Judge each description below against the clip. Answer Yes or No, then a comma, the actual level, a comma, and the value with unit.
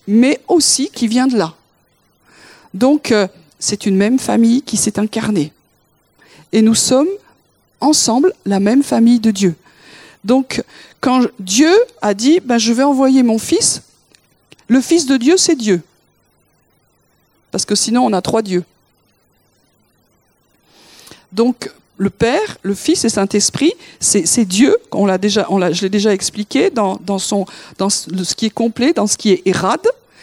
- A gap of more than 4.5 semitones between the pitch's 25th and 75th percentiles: Yes, average, 5.2 semitones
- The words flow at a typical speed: Yes, average, 160 wpm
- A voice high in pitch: Yes, high, 220 Hz